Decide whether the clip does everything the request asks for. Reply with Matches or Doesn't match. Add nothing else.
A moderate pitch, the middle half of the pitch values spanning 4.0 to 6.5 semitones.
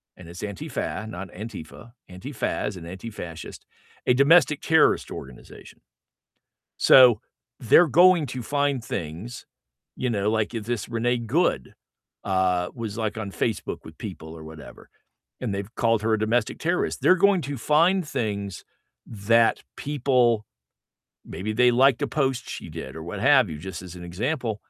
Doesn't match